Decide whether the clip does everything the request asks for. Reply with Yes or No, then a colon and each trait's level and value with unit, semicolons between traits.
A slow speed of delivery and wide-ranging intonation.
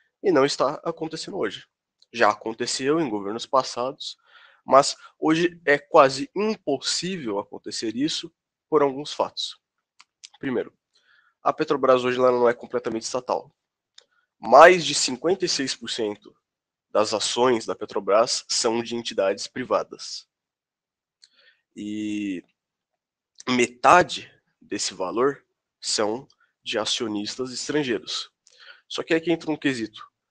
Yes: slow, 105 wpm; wide, 5.7 semitones